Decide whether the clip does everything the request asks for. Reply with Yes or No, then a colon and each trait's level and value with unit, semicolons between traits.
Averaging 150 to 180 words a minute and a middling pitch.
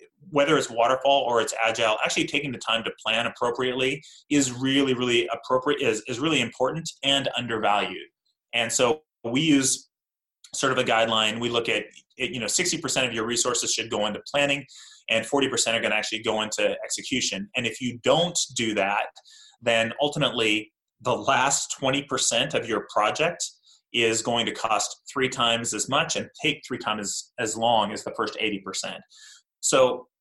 No: average, 175 wpm; low, 125 Hz